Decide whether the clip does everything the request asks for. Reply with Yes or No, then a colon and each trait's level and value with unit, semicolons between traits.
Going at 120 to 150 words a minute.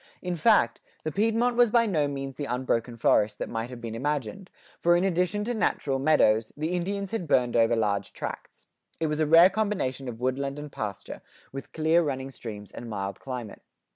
No: average, 195 wpm